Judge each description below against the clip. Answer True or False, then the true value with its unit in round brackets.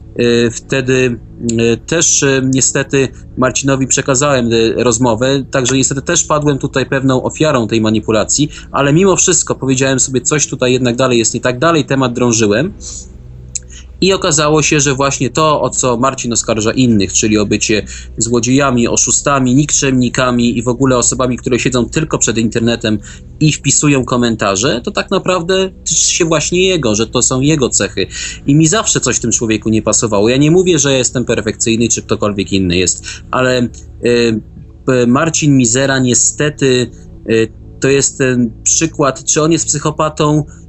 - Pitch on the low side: True (125 Hz)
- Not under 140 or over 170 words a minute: True (155 wpm)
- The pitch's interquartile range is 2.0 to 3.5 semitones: False (3.9 semitones)